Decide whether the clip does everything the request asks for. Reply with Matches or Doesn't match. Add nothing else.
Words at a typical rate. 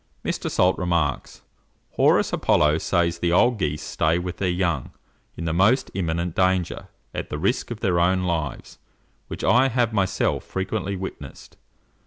Matches